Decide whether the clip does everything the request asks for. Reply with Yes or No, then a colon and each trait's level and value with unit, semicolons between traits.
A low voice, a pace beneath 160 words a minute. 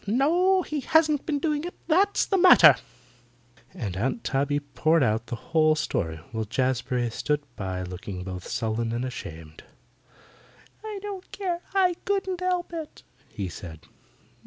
No: medium, 150 Hz; average, 145 wpm